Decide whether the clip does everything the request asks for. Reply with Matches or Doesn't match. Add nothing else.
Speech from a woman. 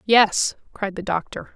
Matches